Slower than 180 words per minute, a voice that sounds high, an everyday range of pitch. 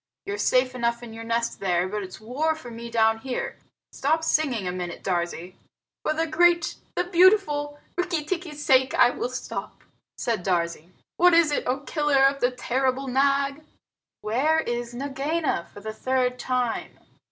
Yes: average, 165 wpm; very high, 260 Hz; average, 5.0 semitones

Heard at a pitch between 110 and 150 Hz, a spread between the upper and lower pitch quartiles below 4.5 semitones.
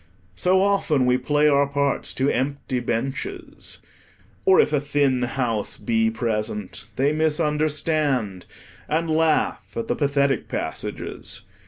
Yes: medium, 140 Hz; average, 3.8 semitones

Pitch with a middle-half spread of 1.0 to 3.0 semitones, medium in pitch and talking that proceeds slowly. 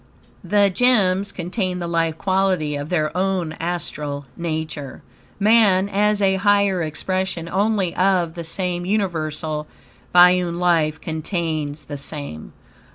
No: average, 3.5 semitones; medium, 175 Hz; slow, 120 wpm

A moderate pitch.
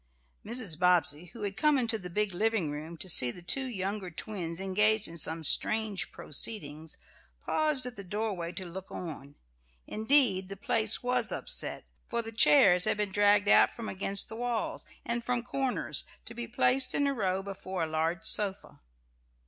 No: high, 200 Hz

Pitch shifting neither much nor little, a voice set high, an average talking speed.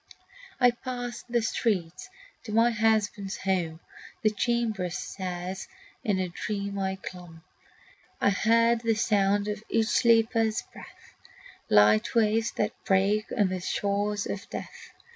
No: average, 3.0 semitones; high, 210 Hz; slow, 130 wpm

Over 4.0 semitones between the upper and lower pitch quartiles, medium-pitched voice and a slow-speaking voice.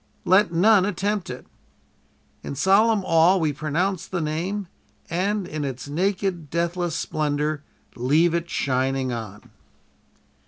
Yes: average, 4.5 semitones; medium, 170 Hz; slow, 120 wpm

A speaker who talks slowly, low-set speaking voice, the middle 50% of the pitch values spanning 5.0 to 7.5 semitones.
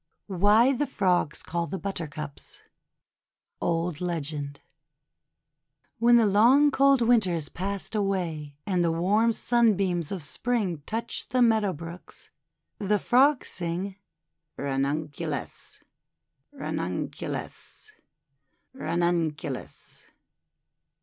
No: slow, 95 wpm; medium, 180 Hz; wide, 5.5 semitones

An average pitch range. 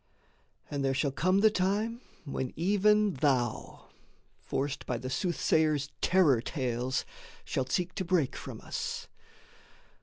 No: wide, 6.2 semitones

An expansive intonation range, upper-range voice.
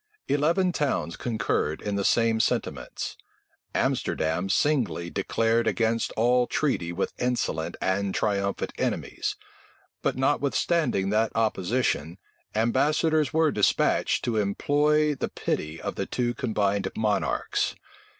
No: wide, 5.9 semitones; low, 115 Hz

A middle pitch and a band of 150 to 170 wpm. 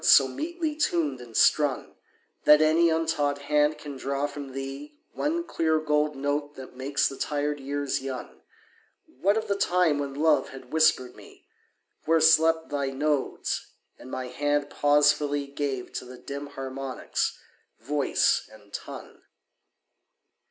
No: medium, 145 Hz; average, 140 wpm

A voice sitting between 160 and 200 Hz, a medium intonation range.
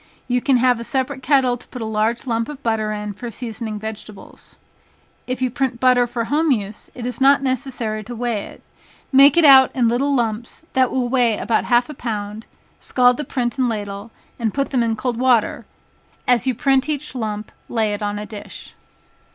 No: high, 240 Hz; average, 3.0 semitones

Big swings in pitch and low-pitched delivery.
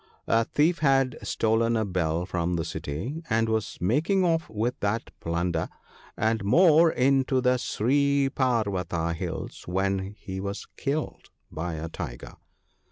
Yes: wide, 7.1 semitones; low, 110 Hz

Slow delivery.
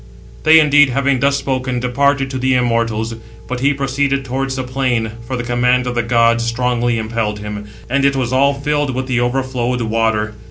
No: average, 190 wpm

